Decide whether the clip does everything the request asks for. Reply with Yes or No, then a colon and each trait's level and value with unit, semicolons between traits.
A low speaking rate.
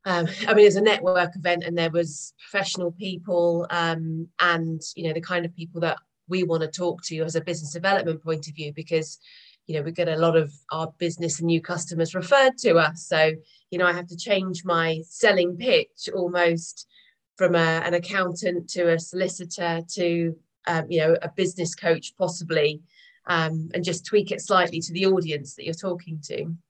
No: average, 200 wpm